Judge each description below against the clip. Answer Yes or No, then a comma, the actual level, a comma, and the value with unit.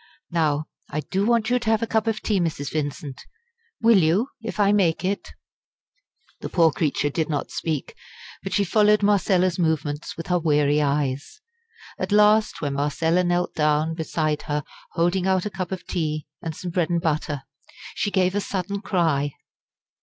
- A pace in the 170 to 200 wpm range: Yes, average, 175 wpm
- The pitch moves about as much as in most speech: Yes, average, 4.8 semitones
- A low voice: No, medium, 170 Hz